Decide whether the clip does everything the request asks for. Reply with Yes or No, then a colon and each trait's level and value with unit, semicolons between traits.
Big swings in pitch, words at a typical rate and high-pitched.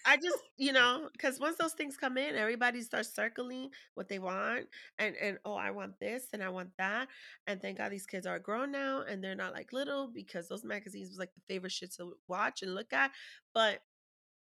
No: wide, 6.1 semitones; fast, 220 wpm; high, 220 Hz